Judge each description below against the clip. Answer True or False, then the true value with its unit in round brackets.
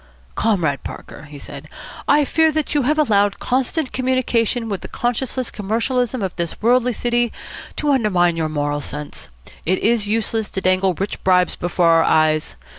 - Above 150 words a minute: True (165 wpm)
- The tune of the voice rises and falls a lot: True (6.1 semitones)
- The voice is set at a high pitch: True (215 Hz)